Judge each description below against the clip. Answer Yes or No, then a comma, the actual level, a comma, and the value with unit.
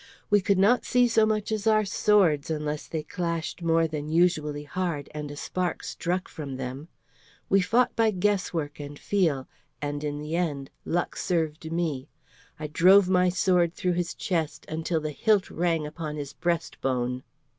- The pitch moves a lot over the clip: No, average, 3.7 semitones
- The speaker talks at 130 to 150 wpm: No, average, 170 wpm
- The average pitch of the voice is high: No, medium, 165 Hz